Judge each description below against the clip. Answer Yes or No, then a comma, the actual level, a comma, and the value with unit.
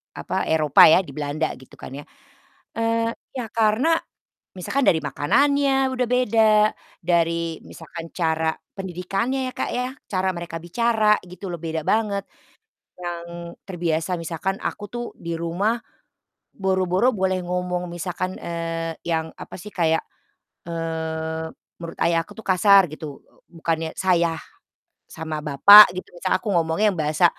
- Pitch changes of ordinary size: Yes, average, 3.9 semitones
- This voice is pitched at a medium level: Yes, medium, 175 Hz